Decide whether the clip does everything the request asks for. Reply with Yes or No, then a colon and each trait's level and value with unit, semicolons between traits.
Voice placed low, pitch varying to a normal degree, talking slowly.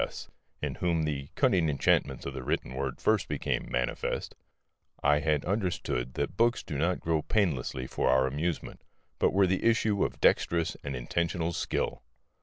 No: very low, 80 Hz; average, 4.5 semitones; average, 165 wpm